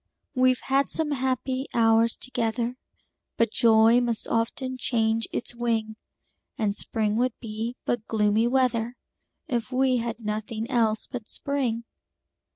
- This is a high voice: Yes, high, 235 Hz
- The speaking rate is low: Yes, slow, 130 wpm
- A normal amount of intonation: No, narrow, 2.3 semitones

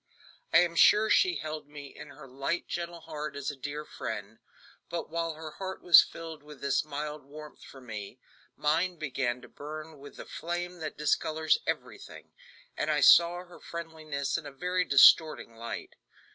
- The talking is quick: No, average, 175 wpm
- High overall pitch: No, medium, 155 Hz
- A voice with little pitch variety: No, average, 3.0 semitones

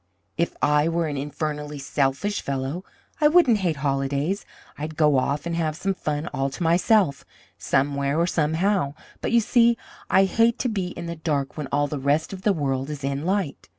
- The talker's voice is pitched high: No, medium, 155 Hz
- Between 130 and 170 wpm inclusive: No, average, 190 wpm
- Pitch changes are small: No, average, 4.8 semitones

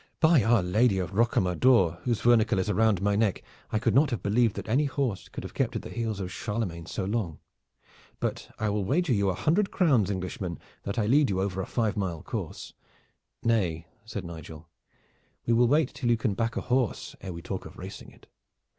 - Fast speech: Yes, fast, 210 wpm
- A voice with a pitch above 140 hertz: No, low, 105 Hz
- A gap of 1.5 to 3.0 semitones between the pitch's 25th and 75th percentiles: No, average, 4.2 semitones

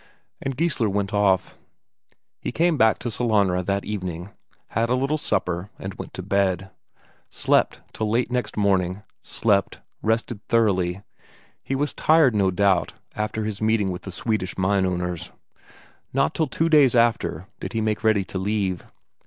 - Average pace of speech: Yes, average, 160 wpm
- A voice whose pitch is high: No, low, 105 Hz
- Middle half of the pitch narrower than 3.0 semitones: No, average, 3.6 semitones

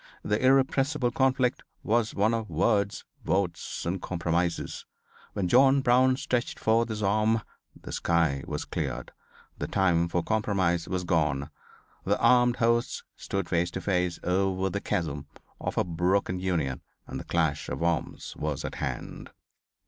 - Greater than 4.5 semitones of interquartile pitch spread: Yes, average, 5.2 semitones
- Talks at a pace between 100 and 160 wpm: Yes, average, 150 wpm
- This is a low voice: Yes, very low, 95 Hz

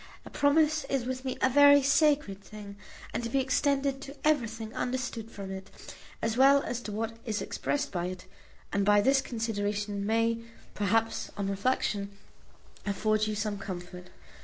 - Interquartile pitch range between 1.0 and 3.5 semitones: No, average, 4.7 semitones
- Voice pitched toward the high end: Yes, high, 225 Hz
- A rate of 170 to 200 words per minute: No, average, 160 wpm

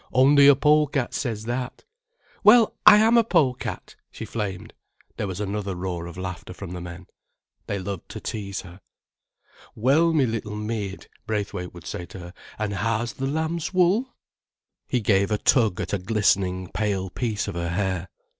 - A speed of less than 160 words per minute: No, average, 175 wpm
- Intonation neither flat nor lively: No, wide, 6.2 semitones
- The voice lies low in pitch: Yes, low, 105 Hz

